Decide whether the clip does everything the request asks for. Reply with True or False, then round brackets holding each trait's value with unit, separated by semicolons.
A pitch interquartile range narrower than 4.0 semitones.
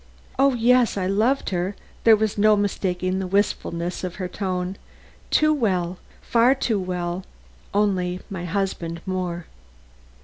True (3.1 semitones)